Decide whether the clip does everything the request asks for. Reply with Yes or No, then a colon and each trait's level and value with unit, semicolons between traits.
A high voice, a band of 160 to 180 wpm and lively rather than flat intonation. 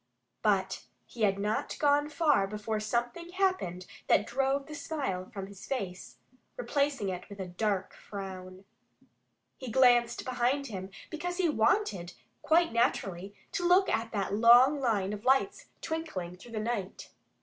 No: high, 230 Hz; average, 150 wpm; wide, 6.3 semitones